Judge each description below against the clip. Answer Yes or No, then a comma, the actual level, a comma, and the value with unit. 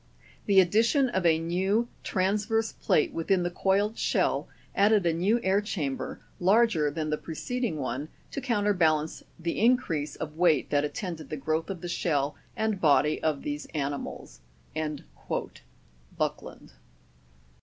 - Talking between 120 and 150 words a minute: Yes, average, 140 wpm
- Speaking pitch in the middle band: Yes, medium, 175 Hz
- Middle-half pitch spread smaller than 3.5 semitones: No, average, 5.2 semitones